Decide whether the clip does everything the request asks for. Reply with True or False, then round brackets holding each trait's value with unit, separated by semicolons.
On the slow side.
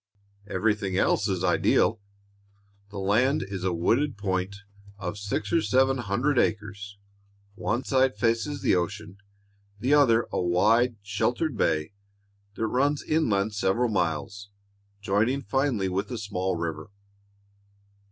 True (125 wpm)